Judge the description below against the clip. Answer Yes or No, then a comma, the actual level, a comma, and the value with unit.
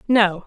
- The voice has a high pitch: Yes, high, 205 Hz